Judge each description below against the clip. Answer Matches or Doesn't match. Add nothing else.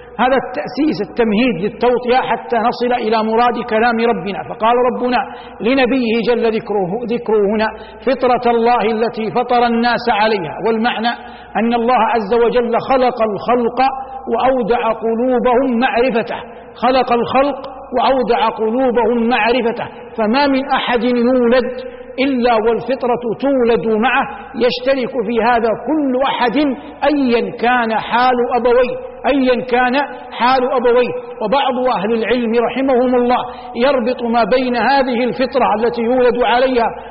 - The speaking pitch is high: Matches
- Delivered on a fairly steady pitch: Matches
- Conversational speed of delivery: Matches